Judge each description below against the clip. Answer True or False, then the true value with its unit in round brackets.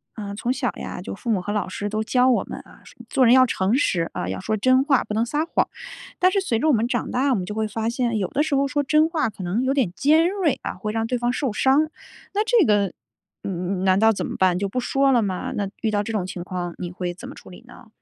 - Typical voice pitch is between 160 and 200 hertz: False (225 Hz)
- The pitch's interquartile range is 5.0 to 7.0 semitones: True (5.3 semitones)